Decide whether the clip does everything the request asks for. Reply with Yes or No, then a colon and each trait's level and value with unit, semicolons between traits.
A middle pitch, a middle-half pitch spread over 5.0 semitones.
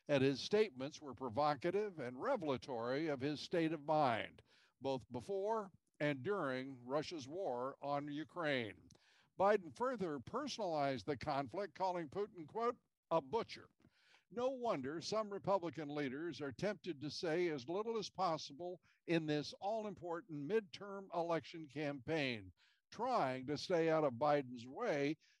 Yes: medium, 160 Hz; wide, 5.4 semitones